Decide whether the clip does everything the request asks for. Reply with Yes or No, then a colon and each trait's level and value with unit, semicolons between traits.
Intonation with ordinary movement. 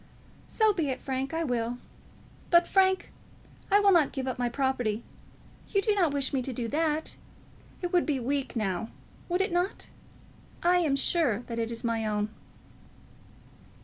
No: wide, 6.5 semitones